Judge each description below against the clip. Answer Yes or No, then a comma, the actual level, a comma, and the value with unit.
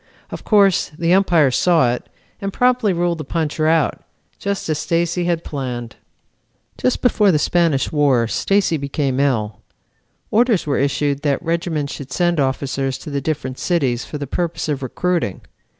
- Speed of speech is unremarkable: Yes, average, 160 wpm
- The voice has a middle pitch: Yes, medium, 155 Hz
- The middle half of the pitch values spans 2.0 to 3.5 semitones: No, average, 4.3 semitones